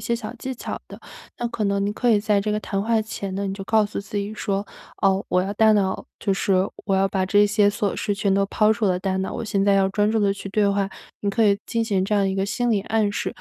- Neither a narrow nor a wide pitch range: No, narrow, 1.5 semitones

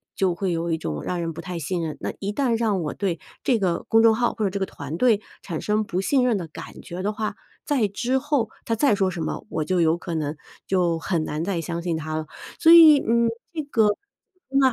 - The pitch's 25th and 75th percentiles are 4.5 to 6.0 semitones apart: Yes, wide, 5.4 semitones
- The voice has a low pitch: No, high, 190 Hz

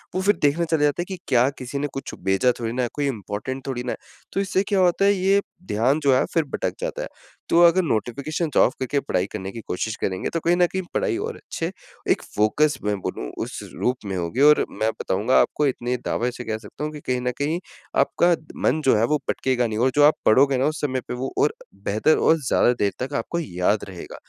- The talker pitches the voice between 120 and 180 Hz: Yes, low, 135 Hz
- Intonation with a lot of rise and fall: Yes, wide, 5.9 semitones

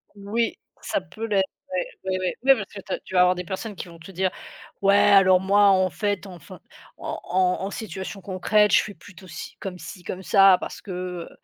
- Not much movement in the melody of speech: Yes, narrow, 1.8 semitones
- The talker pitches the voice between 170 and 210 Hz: Yes, high, 190 Hz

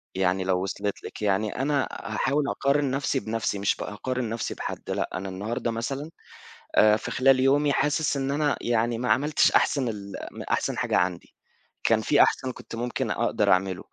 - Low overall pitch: Yes, low, 115 Hz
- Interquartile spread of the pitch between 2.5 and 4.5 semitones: No, average, 5.2 semitones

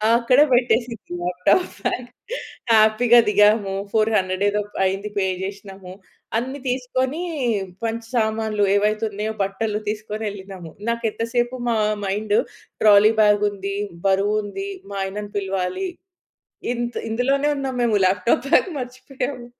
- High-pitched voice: Yes, high, 215 Hz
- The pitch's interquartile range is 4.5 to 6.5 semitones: No, average, 3.2 semitones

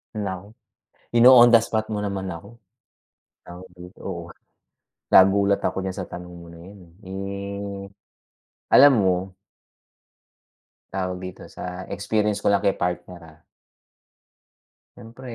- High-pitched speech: No, very low, 95 Hz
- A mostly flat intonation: Yes, narrow, 2.3 semitones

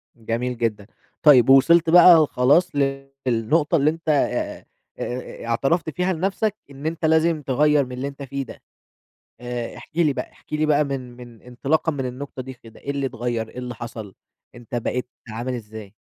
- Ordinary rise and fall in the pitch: Yes, average, 4.2 semitones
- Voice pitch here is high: No, low, 135 Hz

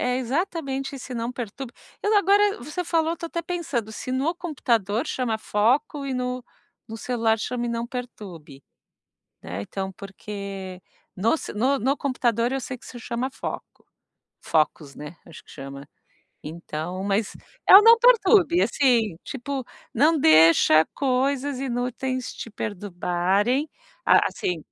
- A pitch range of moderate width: No, wide, 5.9 semitones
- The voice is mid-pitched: No, high, 245 Hz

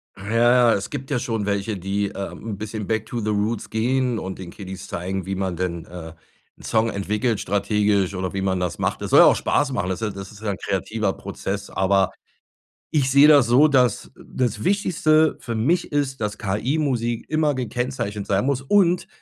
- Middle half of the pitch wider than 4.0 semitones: Yes, average, 4.7 semitones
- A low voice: Yes, low, 110 Hz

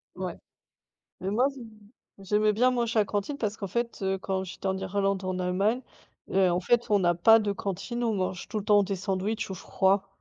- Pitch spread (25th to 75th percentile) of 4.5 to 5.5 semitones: No, average, 2.8 semitones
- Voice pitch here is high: Yes, high, 200 Hz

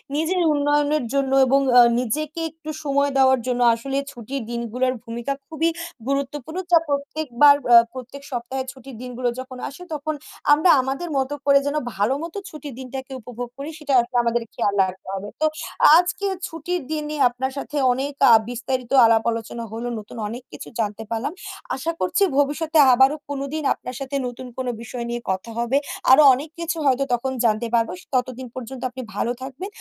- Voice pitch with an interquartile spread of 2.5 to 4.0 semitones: Yes, average, 3.3 semitones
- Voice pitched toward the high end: Yes, very high, 265 Hz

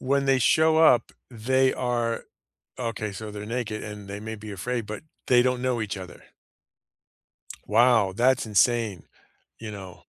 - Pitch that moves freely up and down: No, average, 3.2 semitones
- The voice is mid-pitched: No, low, 115 Hz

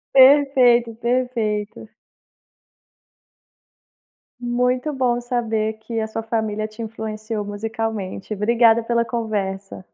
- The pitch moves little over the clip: Yes, narrow, 2.0 semitones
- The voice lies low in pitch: No, high, 225 Hz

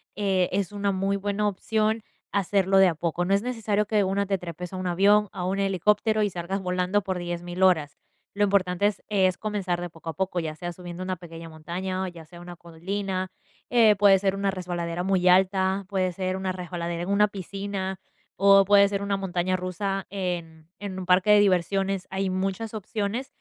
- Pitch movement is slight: Yes, narrow, 2.1 semitones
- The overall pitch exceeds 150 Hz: Yes, high, 190 Hz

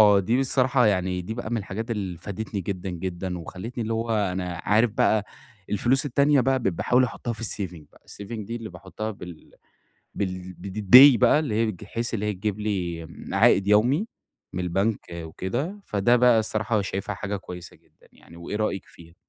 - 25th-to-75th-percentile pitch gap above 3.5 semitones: Yes, average, 4.0 semitones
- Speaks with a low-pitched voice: Yes, low, 105 Hz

